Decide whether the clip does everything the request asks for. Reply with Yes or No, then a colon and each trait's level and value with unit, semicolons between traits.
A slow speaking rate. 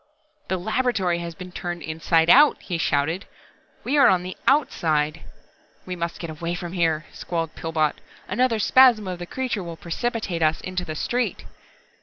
No: average, 165 wpm